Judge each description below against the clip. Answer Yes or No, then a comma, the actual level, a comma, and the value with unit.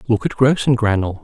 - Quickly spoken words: No, average, 145 wpm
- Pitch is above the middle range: No, low, 120 Hz